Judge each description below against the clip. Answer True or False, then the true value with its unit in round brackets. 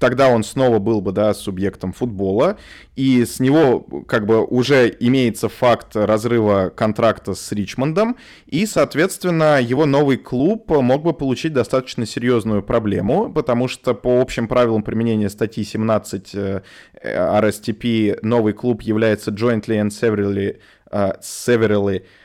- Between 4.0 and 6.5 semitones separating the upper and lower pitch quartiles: False (3.2 semitones)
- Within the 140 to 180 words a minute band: False (130 wpm)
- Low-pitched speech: True (115 Hz)